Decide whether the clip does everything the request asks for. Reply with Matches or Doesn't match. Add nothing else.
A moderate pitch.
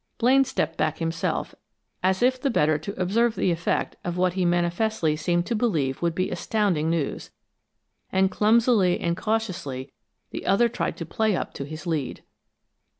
Matches